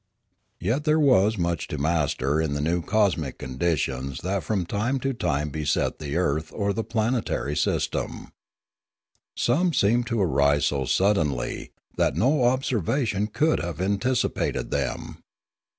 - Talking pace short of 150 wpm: Yes, slow, 135 wpm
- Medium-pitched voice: No, very low, 90 Hz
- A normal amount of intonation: No, wide, 7.7 semitones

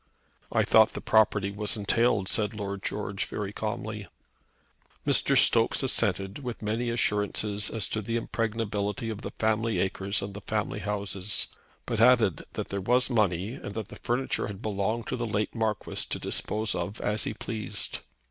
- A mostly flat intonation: Yes, narrow, 2.1 semitones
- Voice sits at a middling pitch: No, low, 105 Hz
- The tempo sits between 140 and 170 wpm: Yes, average, 165 wpm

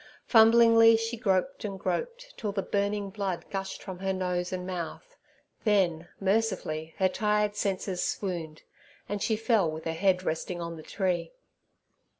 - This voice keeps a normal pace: Yes, average, 155 wpm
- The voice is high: Yes, high, 195 Hz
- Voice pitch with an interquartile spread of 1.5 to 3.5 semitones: Yes, average, 3.2 semitones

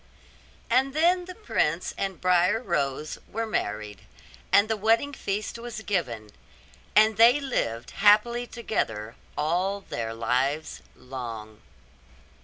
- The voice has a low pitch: No, high, 195 Hz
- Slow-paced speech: Yes, slow, 115 wpm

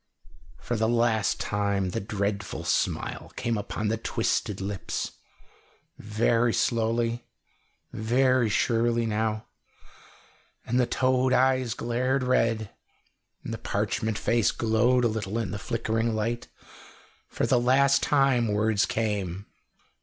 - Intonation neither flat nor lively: No, narrow, 2.2 semitones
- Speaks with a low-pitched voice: Yes, low, 115 Hz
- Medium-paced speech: No, slow, 120 wpm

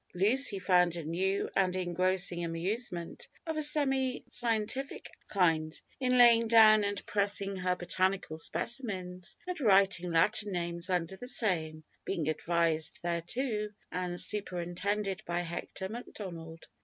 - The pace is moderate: No, slow, 125 wpm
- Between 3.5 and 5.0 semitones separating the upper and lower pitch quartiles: Yes, average, 3.8 semitones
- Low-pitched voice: No, high, 190 Hz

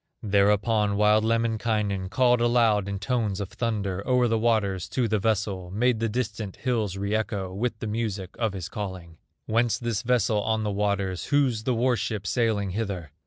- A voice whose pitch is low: Yes, low, 110 Hz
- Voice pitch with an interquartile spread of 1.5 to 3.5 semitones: Yes, average, 2.7 semitones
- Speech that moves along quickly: No, average, 175 wpm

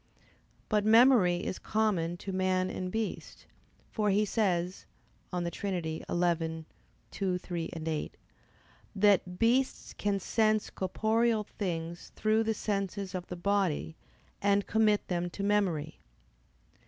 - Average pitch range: Yes, average, 3.3 semitones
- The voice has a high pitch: Yes, high, 195 Hz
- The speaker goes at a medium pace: No, slow, 120 wpm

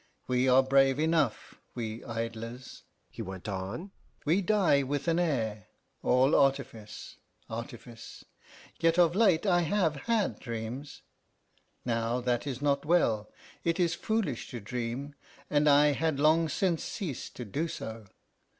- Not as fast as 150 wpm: Yes, average, 140 wpm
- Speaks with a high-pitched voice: No, low, 135 Hz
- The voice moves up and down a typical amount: No, wide, 5.9 semitones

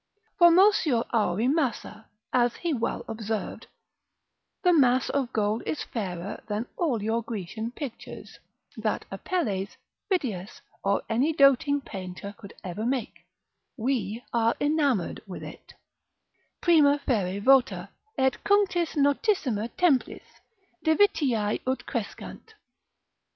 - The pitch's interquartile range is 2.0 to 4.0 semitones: No, wide, 5.5 semitones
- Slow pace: Yes, slow, 110 wpm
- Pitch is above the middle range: Yes, high, 245 Hz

